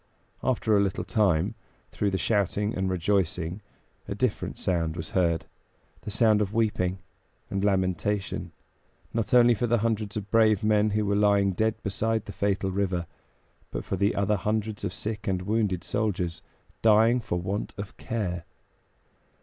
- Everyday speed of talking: Yes, average, 160 wpm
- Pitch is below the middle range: Yes, low, 100 Hz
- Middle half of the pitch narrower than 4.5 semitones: Yes, narrow, 2.5 semitones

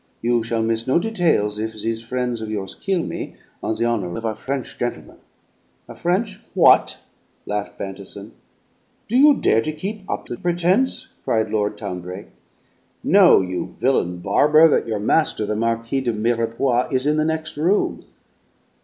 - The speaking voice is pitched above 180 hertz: No, low, 115 Hz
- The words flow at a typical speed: Yes, average, 160 wpm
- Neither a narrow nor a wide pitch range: No, wide, 6.5 semitones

